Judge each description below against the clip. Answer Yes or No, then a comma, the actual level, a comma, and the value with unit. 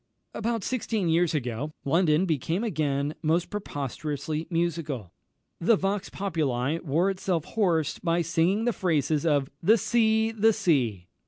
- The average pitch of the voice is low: No, medium, 165 Hz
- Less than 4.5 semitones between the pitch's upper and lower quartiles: No, average, 4.9 semitones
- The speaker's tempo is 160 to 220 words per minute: No, slow, 135 wpm